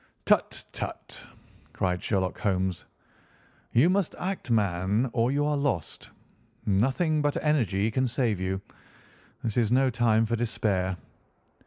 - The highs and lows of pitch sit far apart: Yes, wide, 5.7 semitones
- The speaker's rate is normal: No, slow, 130 wpm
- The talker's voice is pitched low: Yes, low, 115 Hz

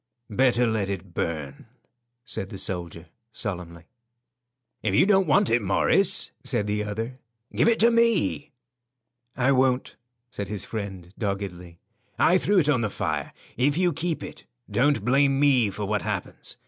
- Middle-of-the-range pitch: No, low, 110 Hz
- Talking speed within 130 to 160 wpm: Yes, average, 155 wpm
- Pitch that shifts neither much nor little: No, wide, 6.4 semitones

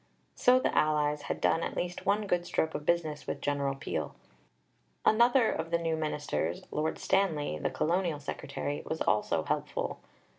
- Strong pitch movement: No, average, 3.3 semitones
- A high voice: No, medium, 155 Hz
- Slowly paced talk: No, average, 160 wpm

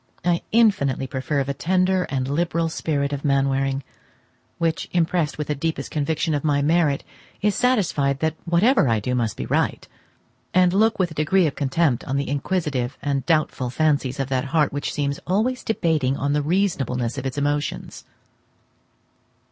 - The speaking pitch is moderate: Yes, medium, 145 Hz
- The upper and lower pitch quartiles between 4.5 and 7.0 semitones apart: No, average, 3.8 semitones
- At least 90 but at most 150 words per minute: No, average, 165 wpm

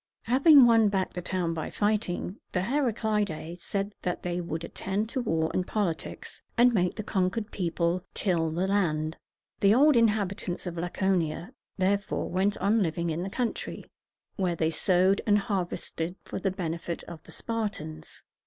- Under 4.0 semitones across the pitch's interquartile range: Yes, average, 3.6 semitones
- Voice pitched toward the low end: No, medium, 185 Hz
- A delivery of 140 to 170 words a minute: Yes, average, 160 wpm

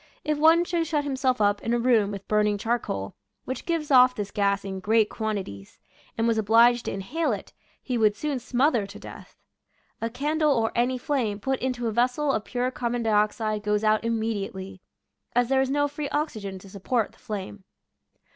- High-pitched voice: Yes, high, 230 Hz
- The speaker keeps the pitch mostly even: No, average, 4.2 semitones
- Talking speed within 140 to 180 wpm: No, average, 195 wpm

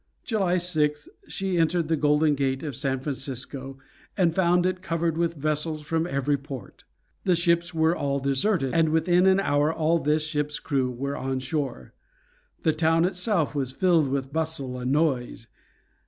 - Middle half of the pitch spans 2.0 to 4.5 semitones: Yes, average, 3.5 semitones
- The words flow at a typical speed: Yes, average, 165 wpm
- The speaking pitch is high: No, medium, 155 Hz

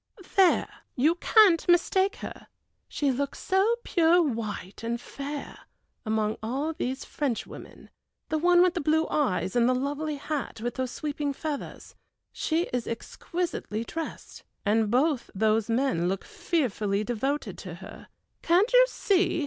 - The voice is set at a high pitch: Yes, very high, 280 Hz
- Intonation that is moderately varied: No, wide, 6.3 semitones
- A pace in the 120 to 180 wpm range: Yes, average, 140 wpm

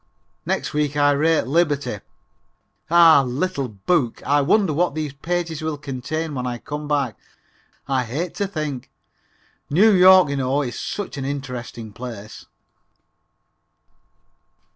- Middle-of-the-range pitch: Yes, medium, 145 Hz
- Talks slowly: Yes, slow, 130 wpm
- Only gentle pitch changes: No, average, 4.1 semitones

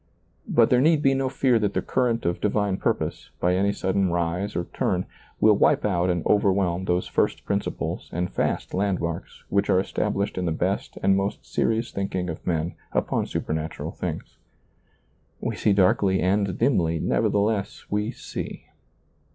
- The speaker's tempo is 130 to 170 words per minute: Yes, average, 165 wpm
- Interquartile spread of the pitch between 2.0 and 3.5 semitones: Yes, average, 2.8 semitones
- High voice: No, very low, 95 Hz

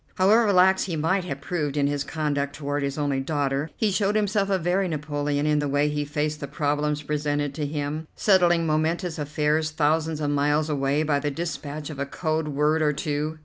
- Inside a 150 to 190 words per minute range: No, average, 200 wpm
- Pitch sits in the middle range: Yes, medium, 150 Hz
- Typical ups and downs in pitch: No, narrow, 1.9 semitones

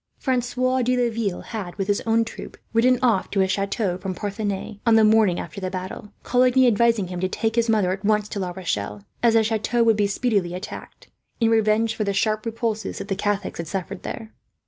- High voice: Yes, high, 215 Hz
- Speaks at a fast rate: Yes, fast, 215 wpm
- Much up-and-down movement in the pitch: No, average, 3.0 semitones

